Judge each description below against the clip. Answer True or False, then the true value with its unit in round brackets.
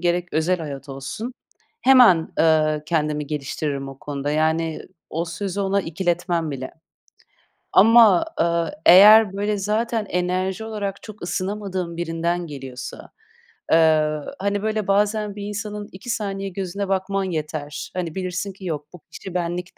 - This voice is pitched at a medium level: True (180 Hz)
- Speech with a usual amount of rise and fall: True (4.0 semitones)